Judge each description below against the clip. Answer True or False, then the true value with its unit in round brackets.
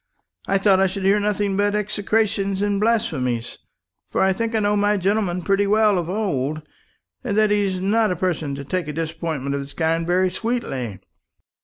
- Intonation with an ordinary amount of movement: True (4.1 semitones)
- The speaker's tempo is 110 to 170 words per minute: False (185 wpm)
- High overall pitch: True (195 Hz)